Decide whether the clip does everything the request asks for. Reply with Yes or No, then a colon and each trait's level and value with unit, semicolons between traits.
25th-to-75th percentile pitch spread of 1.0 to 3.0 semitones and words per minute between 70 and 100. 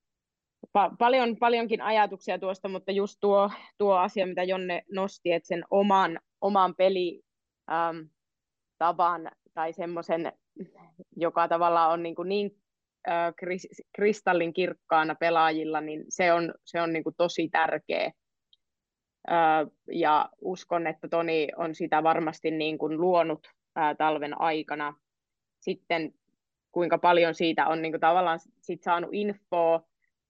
No: narrow, 2.6 semitones; average, 120 wpm